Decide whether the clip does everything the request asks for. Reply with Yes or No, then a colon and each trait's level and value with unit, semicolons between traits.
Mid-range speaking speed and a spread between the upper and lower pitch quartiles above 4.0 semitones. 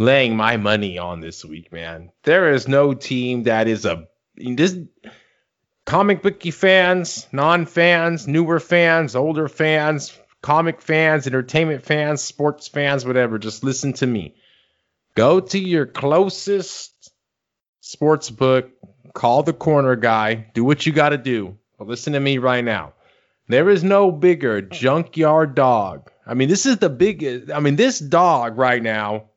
Yes: average, 155 wpm; wide, 5.4 semitones